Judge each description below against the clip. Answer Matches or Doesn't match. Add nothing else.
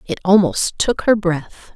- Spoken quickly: Doesn't match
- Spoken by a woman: Matches